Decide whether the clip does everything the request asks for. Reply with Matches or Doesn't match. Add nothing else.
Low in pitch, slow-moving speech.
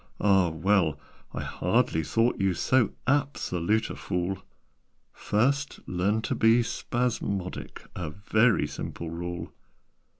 Matches